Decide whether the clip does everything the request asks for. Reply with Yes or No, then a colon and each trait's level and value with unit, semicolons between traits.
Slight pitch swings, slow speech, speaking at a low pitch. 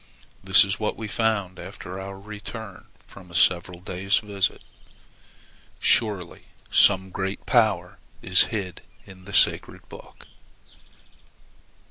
Yes: narrow, 2.3 semitones; slow, 115 wpm; very low, 95 Hz